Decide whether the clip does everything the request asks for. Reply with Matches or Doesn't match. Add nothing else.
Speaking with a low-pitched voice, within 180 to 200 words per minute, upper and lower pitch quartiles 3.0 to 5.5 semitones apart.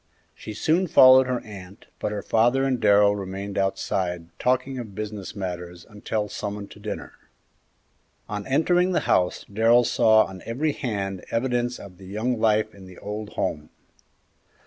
Doesn't match